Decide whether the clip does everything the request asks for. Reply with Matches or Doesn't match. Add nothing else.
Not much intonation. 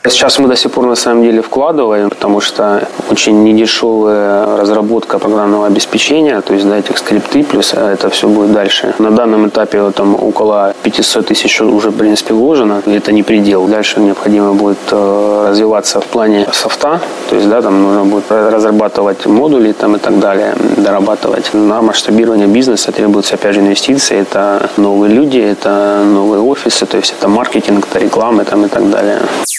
Matches